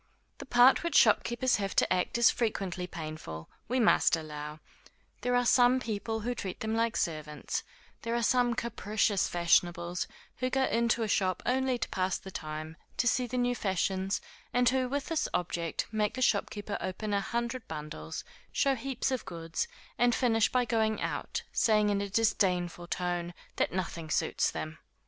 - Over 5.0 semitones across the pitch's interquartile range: Yes, wide, 5.6 semitones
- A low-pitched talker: No, high, 210 Hz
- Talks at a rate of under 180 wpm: Yes, average, 170 wpm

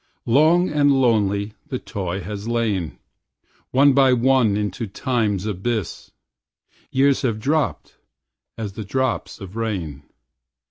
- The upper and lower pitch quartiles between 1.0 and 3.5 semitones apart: No, average, 4.7 semitones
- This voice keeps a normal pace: No, slow, 120 wpm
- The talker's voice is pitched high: No, low, 115 Hz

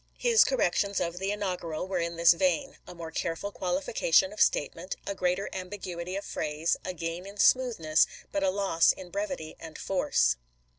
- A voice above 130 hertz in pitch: Yes, medium, 185 Hz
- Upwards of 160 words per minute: Yes, average, 180 wpm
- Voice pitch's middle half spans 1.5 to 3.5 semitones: Yes, average, 3.2 semitones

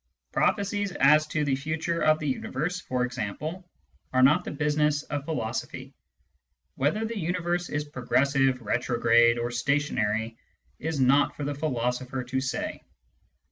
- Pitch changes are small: No, average, 3.8 semitones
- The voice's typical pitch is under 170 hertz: Yes, medium, 140 Hz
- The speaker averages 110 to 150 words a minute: Yes, average, 140 wpm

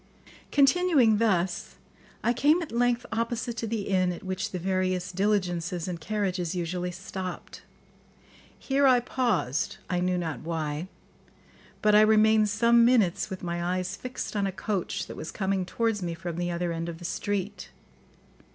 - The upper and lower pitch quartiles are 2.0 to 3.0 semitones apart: No, average, 4.2 semitones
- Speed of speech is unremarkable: Yes, average, 165 wpm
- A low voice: No, high, 190 Hz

